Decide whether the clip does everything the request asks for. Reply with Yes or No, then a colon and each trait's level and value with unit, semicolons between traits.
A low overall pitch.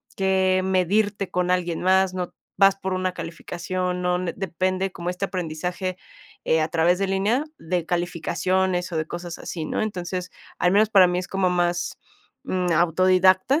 No: medium, 185 Hz